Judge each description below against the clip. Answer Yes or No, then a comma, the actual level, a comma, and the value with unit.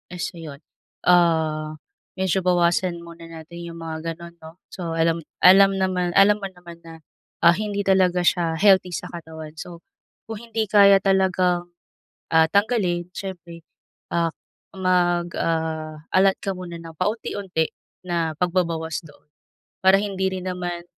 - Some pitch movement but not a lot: No, narrow, 2.3 semitones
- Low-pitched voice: No, medium, 175 Hz